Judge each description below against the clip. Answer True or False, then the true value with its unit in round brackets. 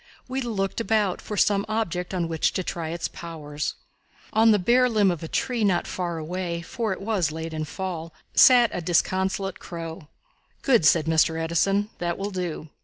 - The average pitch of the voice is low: False (180 Hz)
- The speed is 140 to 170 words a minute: False (185 wpm)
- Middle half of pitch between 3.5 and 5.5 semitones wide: True (4.2 semitones)